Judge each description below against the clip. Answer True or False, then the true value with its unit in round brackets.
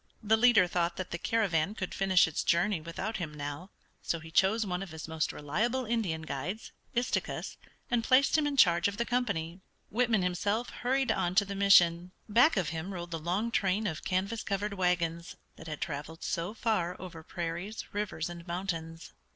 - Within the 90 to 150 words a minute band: False (185 wpm)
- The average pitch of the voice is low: False (185 Hz)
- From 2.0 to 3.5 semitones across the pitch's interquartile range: False (4.3 semitones)